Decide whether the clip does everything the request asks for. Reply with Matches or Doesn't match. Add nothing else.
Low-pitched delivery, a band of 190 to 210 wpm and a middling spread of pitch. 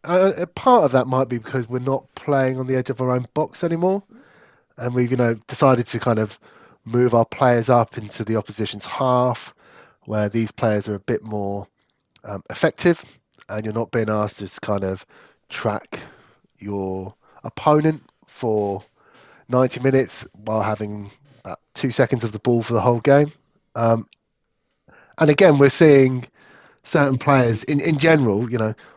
Doesn't match